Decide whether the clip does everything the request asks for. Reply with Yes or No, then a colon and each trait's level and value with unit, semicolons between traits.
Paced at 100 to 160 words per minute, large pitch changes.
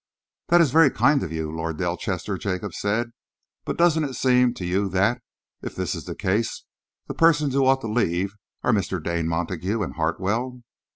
No: average, 185 wpm; wide, 6.6 semitones